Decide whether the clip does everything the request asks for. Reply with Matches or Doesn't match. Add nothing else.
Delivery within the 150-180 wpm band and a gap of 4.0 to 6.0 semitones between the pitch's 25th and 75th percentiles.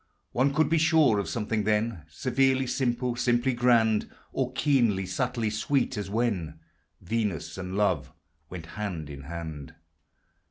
Doesn't match